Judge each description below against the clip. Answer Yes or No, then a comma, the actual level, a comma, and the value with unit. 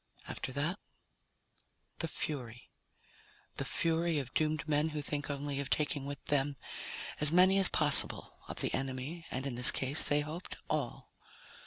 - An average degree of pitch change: No, narrow, 2.3 semitones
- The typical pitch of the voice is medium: Yes, medium, 145 Hz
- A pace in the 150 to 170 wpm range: Yes, average, 155 wpm